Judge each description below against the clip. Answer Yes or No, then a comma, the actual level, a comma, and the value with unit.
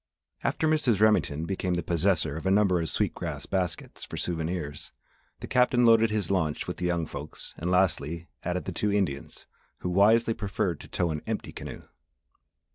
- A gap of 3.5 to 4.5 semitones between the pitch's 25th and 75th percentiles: Yes, average, 4.2 semitones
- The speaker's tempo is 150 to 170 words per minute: No, average, 180 wpm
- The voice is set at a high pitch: No, very low, 90 Hz